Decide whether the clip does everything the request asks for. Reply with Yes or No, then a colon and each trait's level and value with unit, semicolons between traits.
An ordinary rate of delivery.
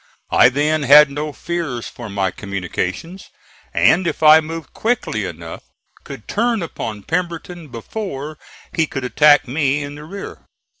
Yes: average, 145 wpm